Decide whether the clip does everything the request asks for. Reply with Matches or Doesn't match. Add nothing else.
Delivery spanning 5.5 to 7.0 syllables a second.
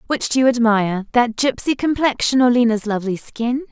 Matches